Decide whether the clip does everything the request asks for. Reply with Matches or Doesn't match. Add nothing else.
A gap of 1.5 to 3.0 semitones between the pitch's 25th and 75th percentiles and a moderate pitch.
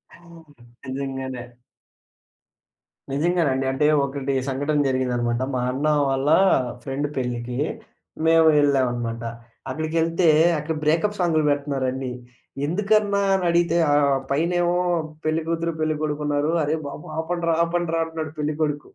Doesn't match